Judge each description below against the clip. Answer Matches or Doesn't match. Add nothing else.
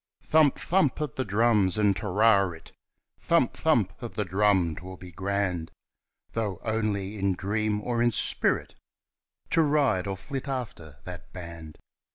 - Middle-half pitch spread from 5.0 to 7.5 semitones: Doesn't match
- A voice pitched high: Doesn't match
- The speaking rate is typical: Matches